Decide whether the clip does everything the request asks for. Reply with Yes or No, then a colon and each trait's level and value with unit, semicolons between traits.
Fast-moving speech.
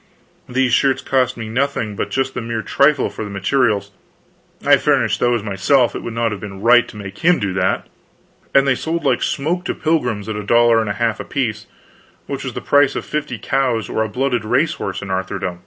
Yes: fast, 215 wpm